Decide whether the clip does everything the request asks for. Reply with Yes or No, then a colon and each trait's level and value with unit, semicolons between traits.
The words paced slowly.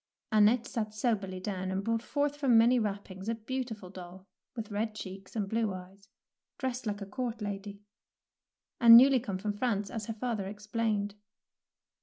No: average, 170 wpm